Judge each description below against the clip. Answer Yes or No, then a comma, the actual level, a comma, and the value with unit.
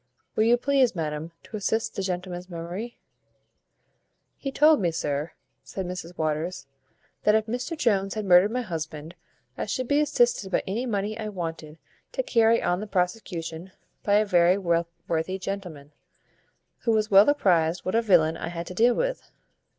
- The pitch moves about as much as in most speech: Yes, average, 4.7 semitones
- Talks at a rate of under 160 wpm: No, average, 165 wpm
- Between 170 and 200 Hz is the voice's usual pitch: Yes, high, 190 Hz